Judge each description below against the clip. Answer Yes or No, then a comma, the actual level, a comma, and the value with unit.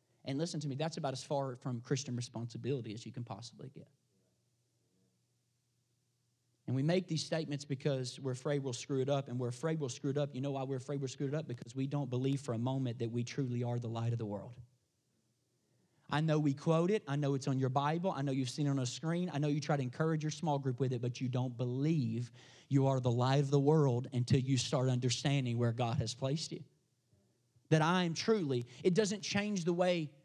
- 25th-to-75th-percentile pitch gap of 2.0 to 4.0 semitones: Yes, average, 3.1 semitones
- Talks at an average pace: No, fast, 235 wpm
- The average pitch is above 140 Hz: No, low, 135 Hz